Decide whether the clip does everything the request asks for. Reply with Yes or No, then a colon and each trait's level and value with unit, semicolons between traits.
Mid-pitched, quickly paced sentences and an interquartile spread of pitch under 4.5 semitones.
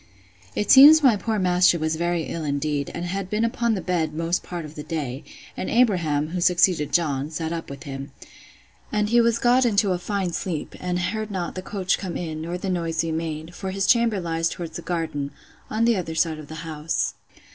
Yes: medium, 175 Hz; fast, 210 wpm; average, 3.8 semitones